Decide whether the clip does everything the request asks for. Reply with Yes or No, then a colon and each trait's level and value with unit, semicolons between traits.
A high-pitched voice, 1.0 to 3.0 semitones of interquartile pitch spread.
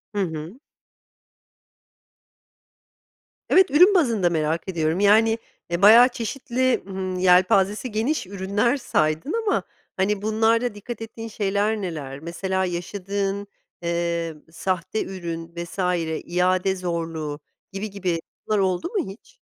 No: high, 195 Hz; average, 4.3 semitones